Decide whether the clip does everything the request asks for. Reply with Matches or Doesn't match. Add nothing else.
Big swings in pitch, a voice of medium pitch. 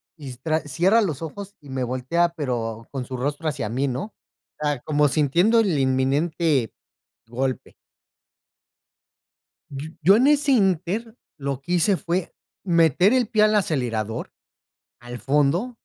Matches